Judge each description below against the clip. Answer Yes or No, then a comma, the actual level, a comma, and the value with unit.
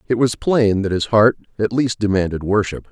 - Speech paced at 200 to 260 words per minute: Yes, fast, 205 wpm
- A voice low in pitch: Yes, low, 110 Hz